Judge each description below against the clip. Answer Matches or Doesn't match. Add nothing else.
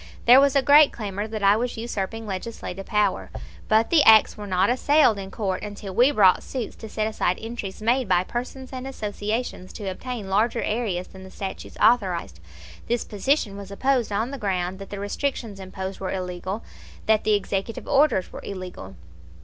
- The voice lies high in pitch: Matches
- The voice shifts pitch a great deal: Doesn't match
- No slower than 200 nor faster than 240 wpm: Doesn't match